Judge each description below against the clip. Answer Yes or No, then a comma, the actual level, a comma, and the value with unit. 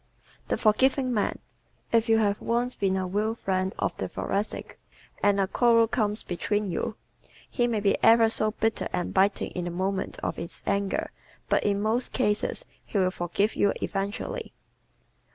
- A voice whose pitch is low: No, high, 210 Hz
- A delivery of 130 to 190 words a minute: Yes, average, 170 wpm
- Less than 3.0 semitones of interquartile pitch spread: Yes, narrow, 2.6 semitones